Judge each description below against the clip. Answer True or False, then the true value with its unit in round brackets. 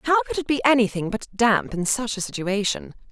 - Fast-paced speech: True (210 wpm)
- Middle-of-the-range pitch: False (230 Hz)